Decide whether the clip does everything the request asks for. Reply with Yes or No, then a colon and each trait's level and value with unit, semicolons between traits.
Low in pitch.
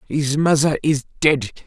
No: medium, 145 Hz